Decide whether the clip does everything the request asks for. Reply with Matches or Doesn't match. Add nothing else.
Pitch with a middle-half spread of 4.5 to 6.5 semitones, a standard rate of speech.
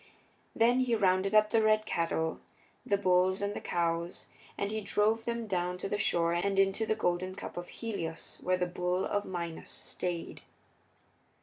Doesn't match